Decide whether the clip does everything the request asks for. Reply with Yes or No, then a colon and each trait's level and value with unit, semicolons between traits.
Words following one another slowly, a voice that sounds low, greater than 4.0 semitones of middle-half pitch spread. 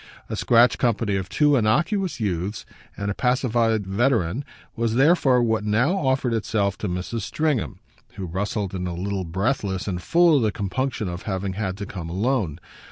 No: average, 170 wpm; low, 110 Hz; average, 4.7 semitones